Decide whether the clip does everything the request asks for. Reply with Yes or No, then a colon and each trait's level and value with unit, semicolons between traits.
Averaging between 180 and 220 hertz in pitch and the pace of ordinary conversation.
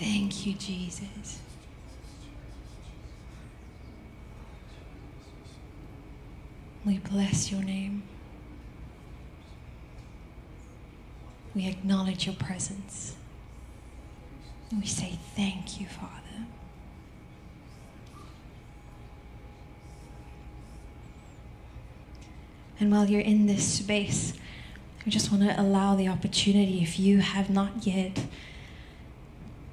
No: high, 190 Hz; slow, 70 wpm